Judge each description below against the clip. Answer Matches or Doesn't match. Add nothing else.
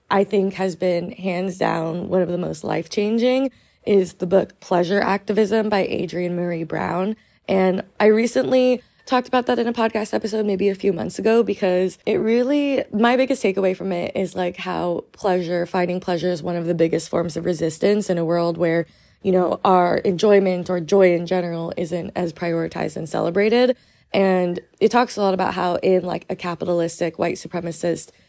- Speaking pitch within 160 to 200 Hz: Matches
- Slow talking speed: Doesn't match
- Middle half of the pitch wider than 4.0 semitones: Doesn't match